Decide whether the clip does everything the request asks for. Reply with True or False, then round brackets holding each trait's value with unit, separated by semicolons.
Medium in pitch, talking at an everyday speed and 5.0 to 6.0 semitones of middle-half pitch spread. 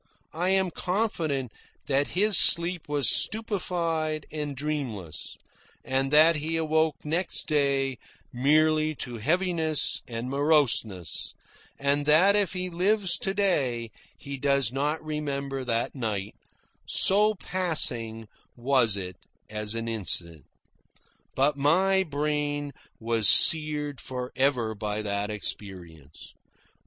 False (145 Hz; 115 wpm; 5.5 semitones)